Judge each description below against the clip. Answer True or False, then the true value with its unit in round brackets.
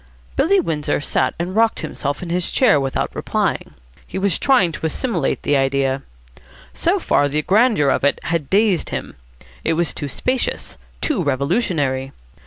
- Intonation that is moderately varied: False (6.5 semitones)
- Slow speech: False (160 wpm)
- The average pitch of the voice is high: False (165 Hz)